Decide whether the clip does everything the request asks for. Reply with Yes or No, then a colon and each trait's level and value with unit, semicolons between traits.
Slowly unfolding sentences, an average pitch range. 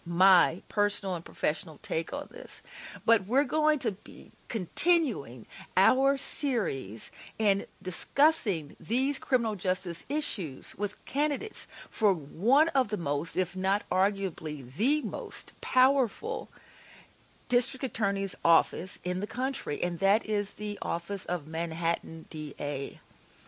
No: slow, 125 wpm; wide, 6.5 semitones